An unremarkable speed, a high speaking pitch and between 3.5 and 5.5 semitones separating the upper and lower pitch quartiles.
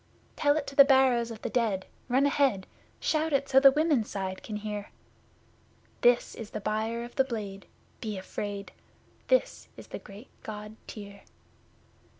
Yes: average, 160 wpm; high, 230 Hz; average, 4.7 semitones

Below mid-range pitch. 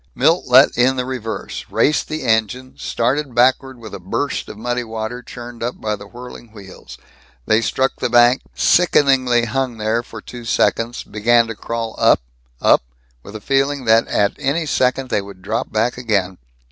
Yes: low, 120 Hz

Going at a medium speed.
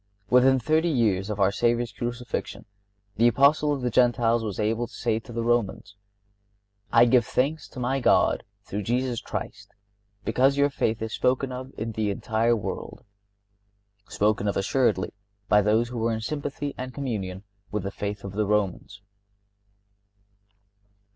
Yes: average, 155 wpm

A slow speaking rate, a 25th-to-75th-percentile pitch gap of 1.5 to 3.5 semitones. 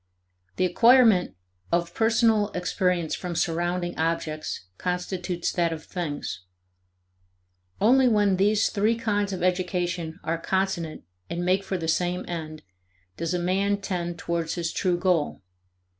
Yes: slow, 130 wpm; narrow, 2.6 semitones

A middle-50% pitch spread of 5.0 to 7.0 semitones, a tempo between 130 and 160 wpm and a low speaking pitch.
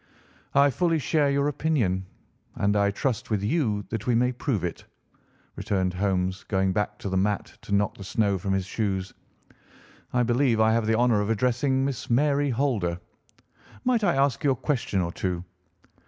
No: wide, 5.6 semitones; average, 180 wpm; low, 110 Hz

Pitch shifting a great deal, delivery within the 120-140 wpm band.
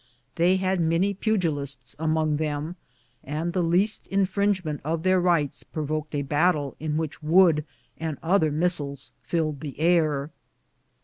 No: average, 3.2 semitones; slow, 135 wpm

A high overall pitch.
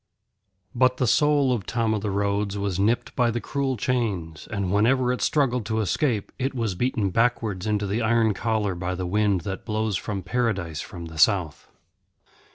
No: low, 110 Hz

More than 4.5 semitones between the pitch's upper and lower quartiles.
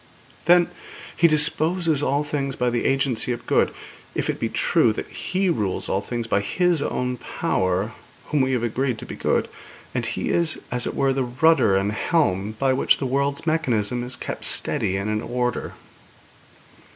Yes: average, 4.9 semitones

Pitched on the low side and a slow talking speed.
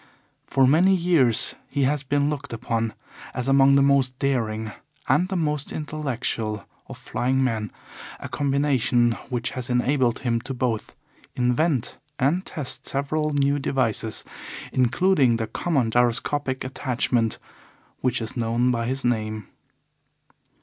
Yes: low, 130 Hz; slow, 130 wpm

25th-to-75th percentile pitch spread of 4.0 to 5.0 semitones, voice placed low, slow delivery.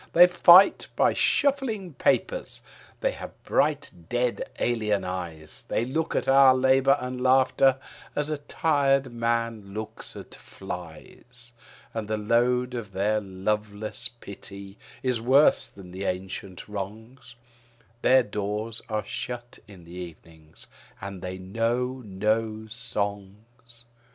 Yes: average, 4.5 semitones; low, 115 Hz; slow, 125 wpm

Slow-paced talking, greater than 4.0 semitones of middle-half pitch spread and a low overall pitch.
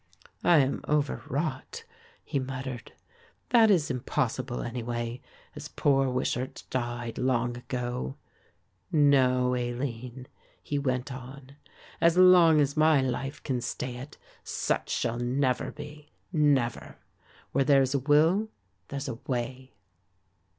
No: slow, 115 wpm; average, 2.9 semitones; low, 130 Hz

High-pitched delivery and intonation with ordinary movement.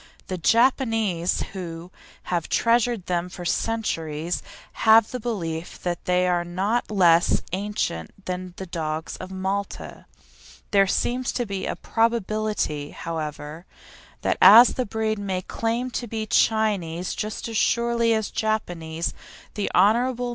Yes: high, 195 Hz; average, 4.4 semitones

